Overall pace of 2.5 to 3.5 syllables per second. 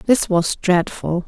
Yes: 3.3 syllables/s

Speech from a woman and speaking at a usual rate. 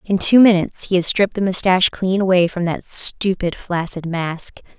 Yes: female; average, 190 wpm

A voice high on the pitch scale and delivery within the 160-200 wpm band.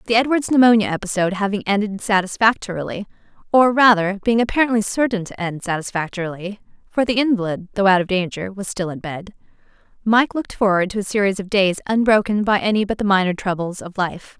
Yes: high, 200 Hz; average, 180 wpm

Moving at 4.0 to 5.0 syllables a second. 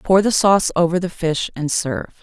No: 5.8 syllables/s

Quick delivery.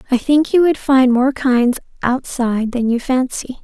No: average, 180 wpm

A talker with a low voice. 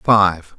Yes: very low, 95 Hz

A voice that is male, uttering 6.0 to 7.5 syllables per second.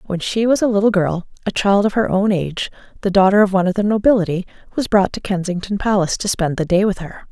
No: female; 6.5 syllables/s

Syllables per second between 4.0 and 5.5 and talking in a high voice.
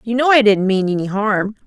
Yes: 5.4 syllables/s; high, 215 Hz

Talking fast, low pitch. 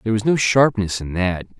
Yes: fast, 225 wpm; low, 105 Hz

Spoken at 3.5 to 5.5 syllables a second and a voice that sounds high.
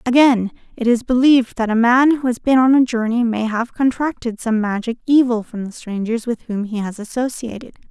Yes: 5.3 syllables/s; high, 235 Hz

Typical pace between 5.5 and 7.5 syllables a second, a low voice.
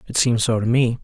Yes: 5.8 syllables/s; low, 120 Hz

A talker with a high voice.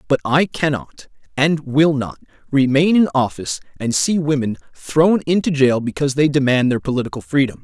No: medium, 145 Hz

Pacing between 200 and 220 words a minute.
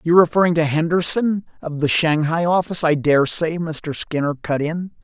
No: average, 180 wpm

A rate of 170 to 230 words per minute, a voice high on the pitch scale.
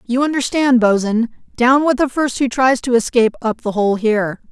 Yes: average, 200 wpm; high, 245 Hz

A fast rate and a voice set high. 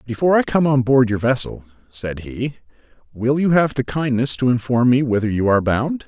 No: fast, 210 wpm; low, 125 Hz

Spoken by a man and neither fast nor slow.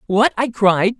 Yes: male; average, 180 wpm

